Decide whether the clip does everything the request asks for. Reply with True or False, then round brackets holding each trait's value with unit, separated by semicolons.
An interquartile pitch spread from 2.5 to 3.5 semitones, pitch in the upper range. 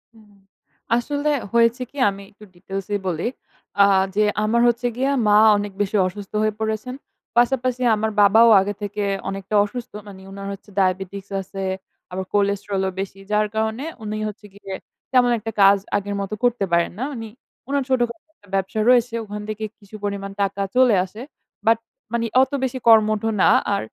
True (3.0 semitones; 210 Hz)